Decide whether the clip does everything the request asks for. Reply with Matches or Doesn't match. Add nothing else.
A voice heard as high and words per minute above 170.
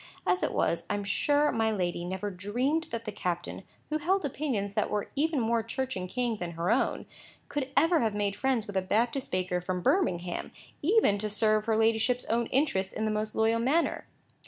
Matches